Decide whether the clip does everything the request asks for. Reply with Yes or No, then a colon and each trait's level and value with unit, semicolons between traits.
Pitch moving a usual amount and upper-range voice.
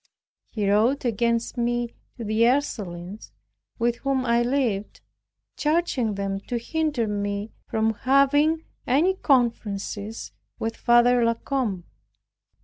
Yes: average, 3.9 semitones; high, 235 Hz